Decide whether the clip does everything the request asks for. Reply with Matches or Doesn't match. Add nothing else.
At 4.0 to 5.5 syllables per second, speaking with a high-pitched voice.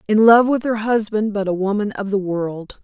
Matches